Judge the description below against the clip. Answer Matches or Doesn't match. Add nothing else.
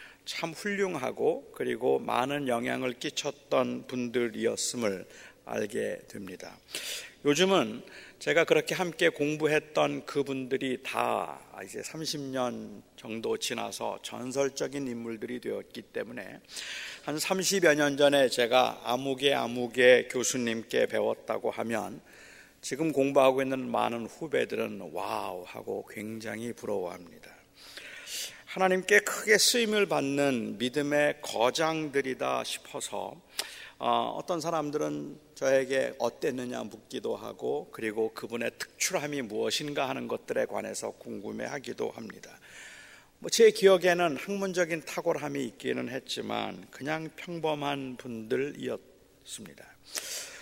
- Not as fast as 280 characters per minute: Matches